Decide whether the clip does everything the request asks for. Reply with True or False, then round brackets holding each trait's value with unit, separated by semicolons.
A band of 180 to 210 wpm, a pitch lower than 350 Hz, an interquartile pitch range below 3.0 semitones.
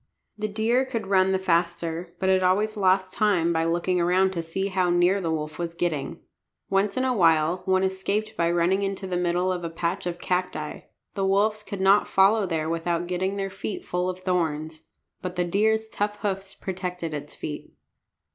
True (195 wpm; 185 Hz; 2.4 semitones)